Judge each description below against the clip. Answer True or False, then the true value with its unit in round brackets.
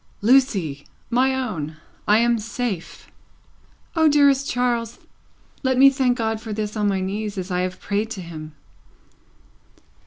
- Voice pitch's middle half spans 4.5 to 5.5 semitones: True (4.9 semitones)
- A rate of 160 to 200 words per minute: False (145 wpm)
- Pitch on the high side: True (220 Hz)